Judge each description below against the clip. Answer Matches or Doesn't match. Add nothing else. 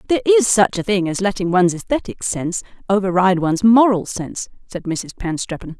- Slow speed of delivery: Doesn't match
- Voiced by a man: Doesn't match